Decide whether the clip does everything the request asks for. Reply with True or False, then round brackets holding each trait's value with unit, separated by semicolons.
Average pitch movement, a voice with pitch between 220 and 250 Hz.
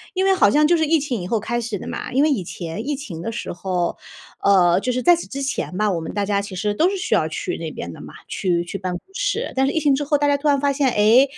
False (6.8 semitones; 245 Hz)